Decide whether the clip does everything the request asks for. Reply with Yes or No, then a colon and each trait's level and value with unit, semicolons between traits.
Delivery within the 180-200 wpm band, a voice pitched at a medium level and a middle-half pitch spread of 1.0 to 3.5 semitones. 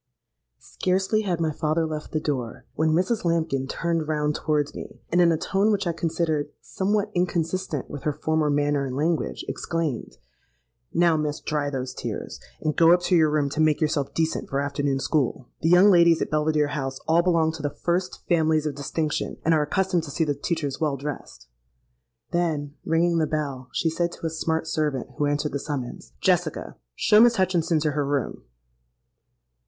Yes: average, 185 wpm; medium, 155 Hz; narrow, 2.6 semitones